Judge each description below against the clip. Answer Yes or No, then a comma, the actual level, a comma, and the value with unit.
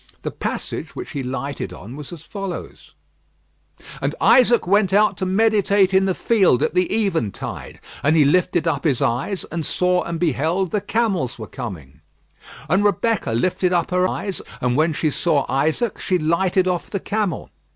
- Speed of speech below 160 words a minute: No, average, 175 wpm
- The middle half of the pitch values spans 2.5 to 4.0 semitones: No, average, 5.0 semitones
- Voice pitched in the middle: Yes, medium, 180 Hz